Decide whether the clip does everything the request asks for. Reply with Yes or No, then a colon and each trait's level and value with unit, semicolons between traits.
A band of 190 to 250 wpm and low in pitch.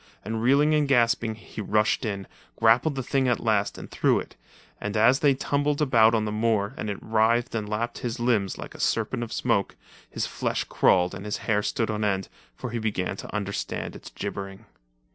Yes: average, 200 wpm; low, 110 Hz